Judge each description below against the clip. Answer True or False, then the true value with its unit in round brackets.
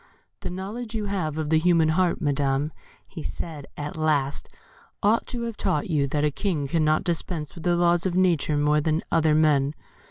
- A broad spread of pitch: False (3.3 semitones)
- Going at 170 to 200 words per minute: True (190 wpm)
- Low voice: False (160 Hz)